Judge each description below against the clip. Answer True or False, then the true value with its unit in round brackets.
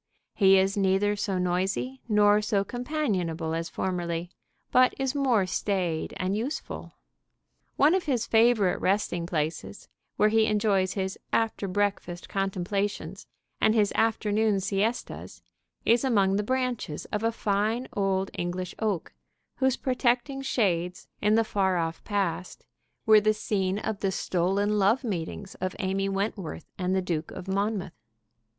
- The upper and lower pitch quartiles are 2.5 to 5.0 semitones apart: True (3.0 semitones)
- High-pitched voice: True (200 Hz)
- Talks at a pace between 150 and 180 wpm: False (140 wpm)